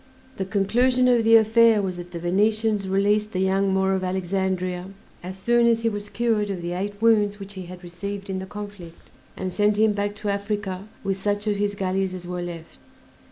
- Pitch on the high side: Yes, high, 200 Hz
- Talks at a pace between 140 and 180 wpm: No, fast, 205 wpm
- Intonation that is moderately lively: No, narrow, 2.0 semitones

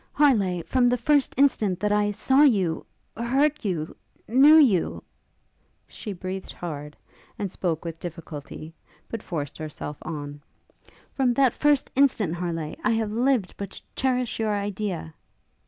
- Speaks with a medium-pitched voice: No, high, 205 Hz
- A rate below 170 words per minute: Yes, average, 145 wpm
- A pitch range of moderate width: No, wide, 7.0 semitones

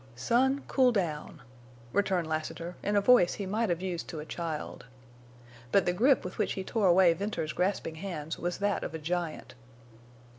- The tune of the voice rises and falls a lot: No, average, 3.8 semitones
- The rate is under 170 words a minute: No, average, 175 wpm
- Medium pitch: Yes, medium, 180 Hz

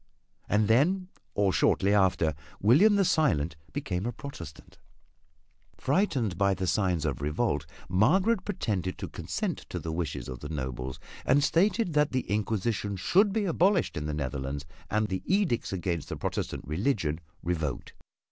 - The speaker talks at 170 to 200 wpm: No, average, 150 wpm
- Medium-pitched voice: No, low, 100 Hz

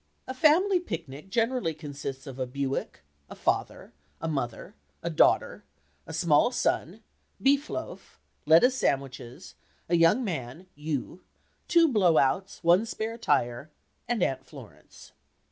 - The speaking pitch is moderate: Yes, medium, 165 Hz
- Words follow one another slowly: Yes, slow, 130 wpm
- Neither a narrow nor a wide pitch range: No, wide, 8.9 semitones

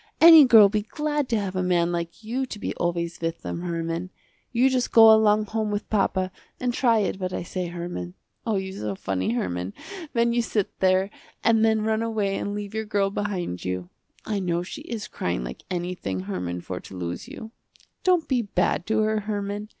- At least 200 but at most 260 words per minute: Yes, fast, 205 wpm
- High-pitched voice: Yes, high, 200 Hz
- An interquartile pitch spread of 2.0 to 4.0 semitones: No, average, 4.4 semitones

